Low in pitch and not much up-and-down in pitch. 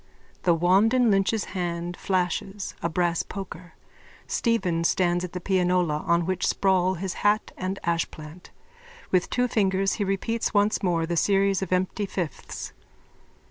No: medium, 185 Hz; narrow, 2.2 semitones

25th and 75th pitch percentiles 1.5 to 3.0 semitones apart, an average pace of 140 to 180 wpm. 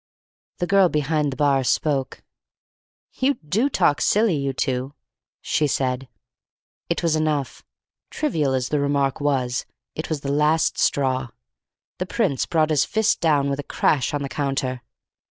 Yes: average, 2.7 semitones; average, 155 wpm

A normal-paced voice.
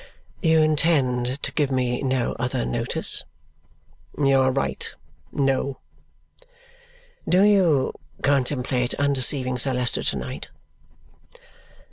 No: slow, 100 wpm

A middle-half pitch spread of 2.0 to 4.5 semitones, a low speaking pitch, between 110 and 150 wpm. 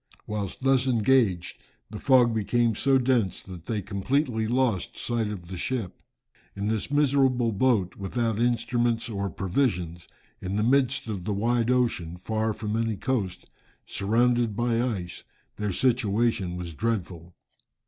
Yes: average, 3.9 semitones; low, 110 Hz; average, 140 wpm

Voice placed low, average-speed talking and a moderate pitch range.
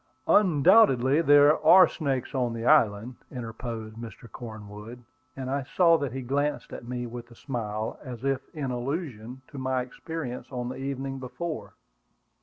Yes: low, 130 Hz; average, 155 wpm; average, 3.2 semitones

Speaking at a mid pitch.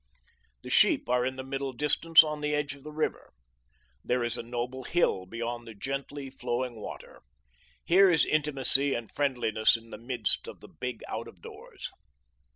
No: low, 130 Hz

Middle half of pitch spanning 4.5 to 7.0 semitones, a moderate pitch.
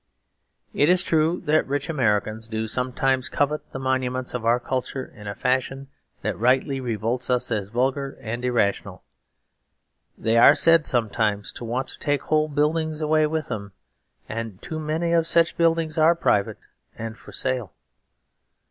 No: average, 5.0 semitones; low, 130 Hz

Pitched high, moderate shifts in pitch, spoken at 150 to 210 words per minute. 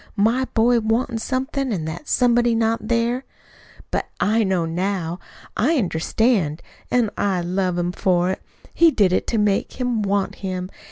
Yes: high, 210 Hz; average, 4.7 semitones; average, 160 wpm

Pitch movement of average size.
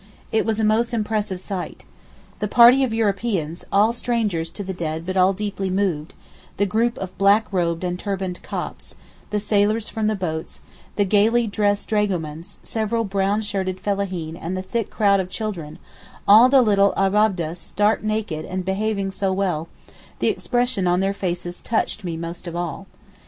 Yes: average, 3.0 semitones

